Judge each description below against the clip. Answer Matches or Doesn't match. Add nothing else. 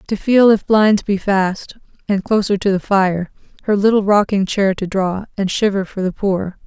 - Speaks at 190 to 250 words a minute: Matches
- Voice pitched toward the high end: Matches